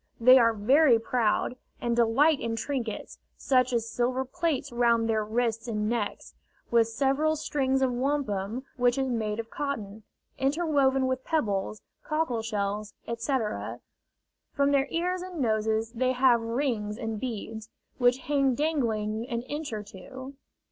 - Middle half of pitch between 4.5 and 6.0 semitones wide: No, average, 3.4 semitones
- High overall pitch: Yes, high, 245 Hz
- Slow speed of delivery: No, average, 145 wpm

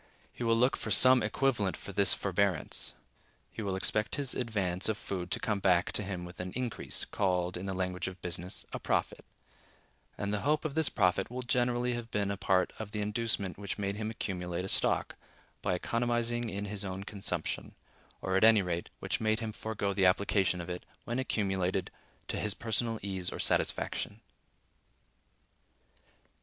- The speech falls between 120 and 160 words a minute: No, average, 180 wpm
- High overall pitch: No, low, 100 Hz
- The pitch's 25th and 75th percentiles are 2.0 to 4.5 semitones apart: Yes, average, 3.5 semitones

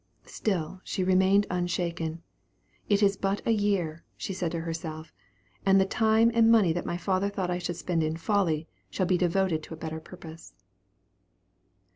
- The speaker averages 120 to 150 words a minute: No, average, 170 wpm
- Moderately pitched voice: Yes, medium, 180 Hz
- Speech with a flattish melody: No, average, 3.2 semitones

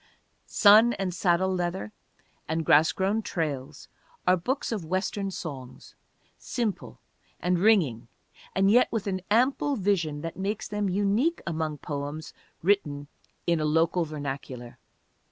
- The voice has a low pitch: No, medium, 180 Hz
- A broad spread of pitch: No, average, 4.9 semitones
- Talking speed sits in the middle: No, slow, 130 wpm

